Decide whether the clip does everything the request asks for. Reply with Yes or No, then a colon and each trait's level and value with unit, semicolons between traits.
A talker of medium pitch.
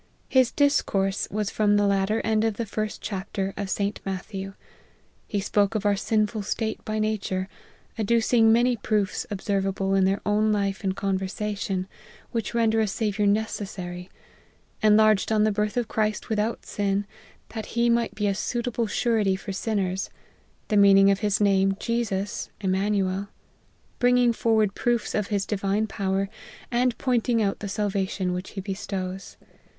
No: high, 205 Hz